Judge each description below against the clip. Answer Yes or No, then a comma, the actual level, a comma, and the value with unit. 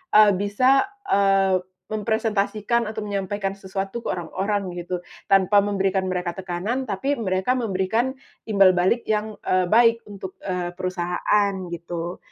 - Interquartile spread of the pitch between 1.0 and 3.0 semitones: Yes, narrow, 2.6 semitones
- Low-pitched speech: No, high, 195 Hz